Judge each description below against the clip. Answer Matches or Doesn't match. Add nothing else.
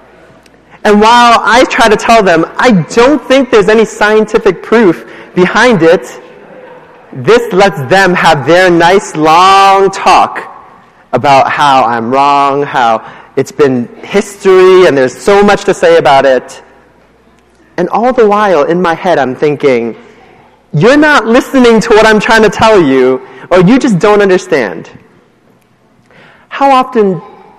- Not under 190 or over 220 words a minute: Doesn't match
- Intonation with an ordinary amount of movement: Doesn't match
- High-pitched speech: Matches